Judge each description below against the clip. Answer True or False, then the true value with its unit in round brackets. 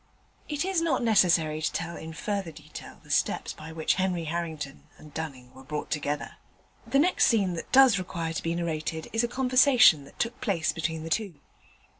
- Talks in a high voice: False (170 Hz)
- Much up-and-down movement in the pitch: True (6.2 semitones)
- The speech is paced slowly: False (190 wpm)